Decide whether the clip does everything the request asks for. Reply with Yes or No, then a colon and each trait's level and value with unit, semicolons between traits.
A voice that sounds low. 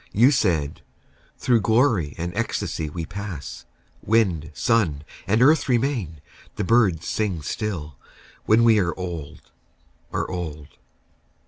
Yes: very low, 95 Hz